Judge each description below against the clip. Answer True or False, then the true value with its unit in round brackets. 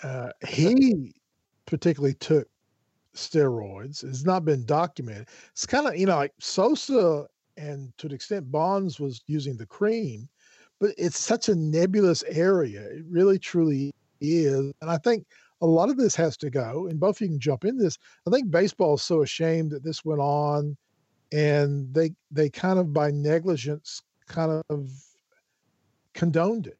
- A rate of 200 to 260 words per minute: False (165 wpm)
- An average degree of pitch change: True (4.2 semitones)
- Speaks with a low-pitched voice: False (155 Hz)